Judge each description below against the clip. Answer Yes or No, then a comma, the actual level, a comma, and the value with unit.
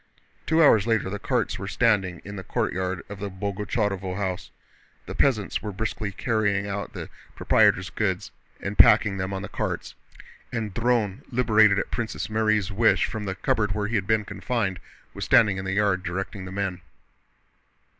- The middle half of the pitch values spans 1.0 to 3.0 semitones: Yes, narrow, 2.4 semitones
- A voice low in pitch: Yes, low, 100 Hz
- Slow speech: No, average, 175 wpm